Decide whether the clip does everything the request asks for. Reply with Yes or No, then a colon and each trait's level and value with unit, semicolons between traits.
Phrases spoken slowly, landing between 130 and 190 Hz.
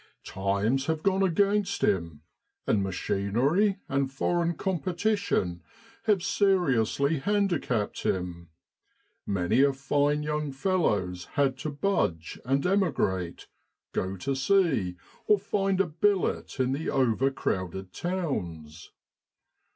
Yes: slow, 110 wpm; medium, 140 Hz